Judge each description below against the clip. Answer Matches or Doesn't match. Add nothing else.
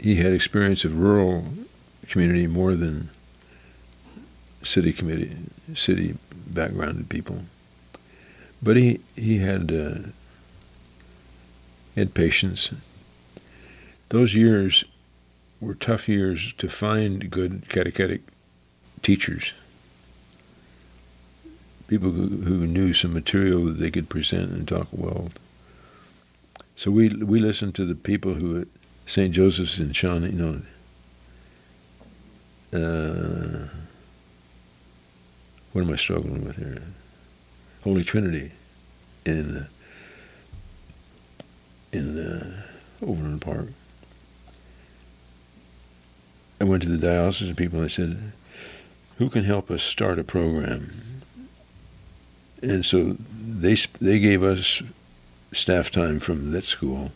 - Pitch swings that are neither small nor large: Doesn't match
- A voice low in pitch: Matches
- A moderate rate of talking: Doesn't match